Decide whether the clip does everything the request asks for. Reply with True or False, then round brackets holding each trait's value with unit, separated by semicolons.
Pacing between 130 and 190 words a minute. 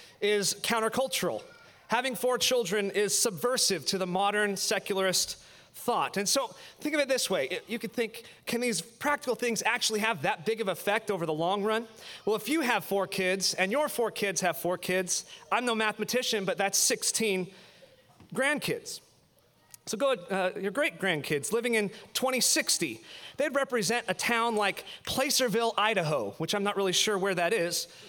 True (170 wpm)